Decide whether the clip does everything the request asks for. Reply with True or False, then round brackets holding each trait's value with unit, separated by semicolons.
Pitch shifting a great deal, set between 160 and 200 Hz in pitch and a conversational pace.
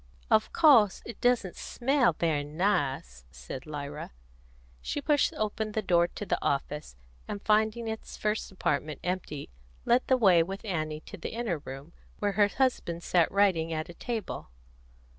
True (6.1 semitones; 185 Hz; 160 wpm)